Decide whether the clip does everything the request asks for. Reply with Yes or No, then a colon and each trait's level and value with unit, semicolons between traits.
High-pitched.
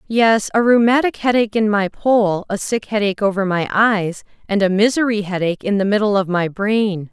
Yes: high, 205 Hz